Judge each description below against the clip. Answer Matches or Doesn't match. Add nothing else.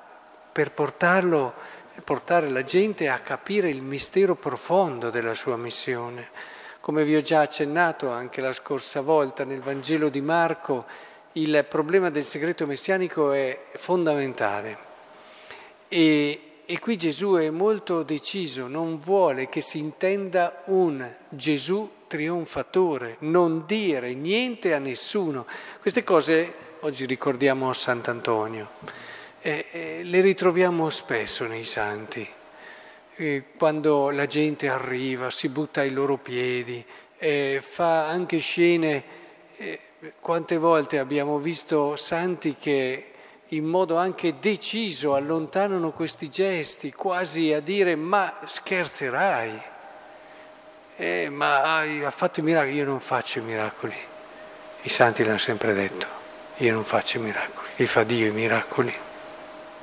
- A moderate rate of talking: Matches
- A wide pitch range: Doesn't match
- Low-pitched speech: Doesn't match